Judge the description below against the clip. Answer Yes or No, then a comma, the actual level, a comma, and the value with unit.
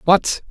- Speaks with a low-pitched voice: No, medium, 185 Hz